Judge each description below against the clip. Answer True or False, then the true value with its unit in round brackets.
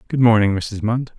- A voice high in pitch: False (110 Hz)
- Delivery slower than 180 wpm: False (205 wpm)